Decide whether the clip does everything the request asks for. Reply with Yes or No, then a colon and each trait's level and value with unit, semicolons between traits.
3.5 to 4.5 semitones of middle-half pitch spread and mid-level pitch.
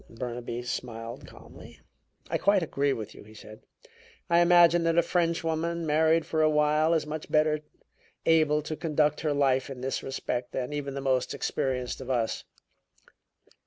Yes: average, 4.0 semitones; medium, 150 Hz